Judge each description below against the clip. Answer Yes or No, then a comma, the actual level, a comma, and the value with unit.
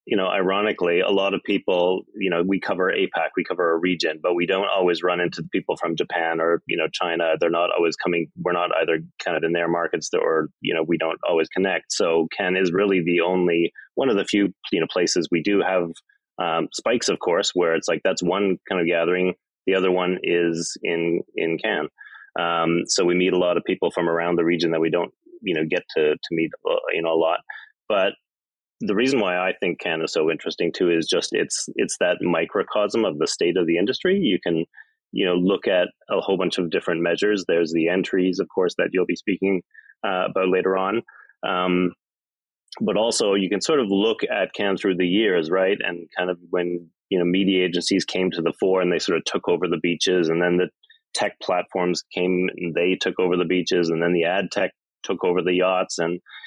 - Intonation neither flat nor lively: No, narrow, 2.3 semitones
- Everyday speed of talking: No, fast, 225 wpm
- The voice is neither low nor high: No, very low, 90 Hz